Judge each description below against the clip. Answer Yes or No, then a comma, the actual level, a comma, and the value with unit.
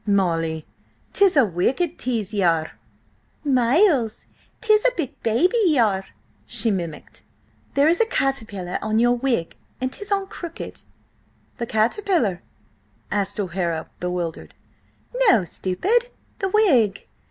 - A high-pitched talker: Yes, high, 235 Hz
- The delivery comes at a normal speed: No, slow, 125 wpm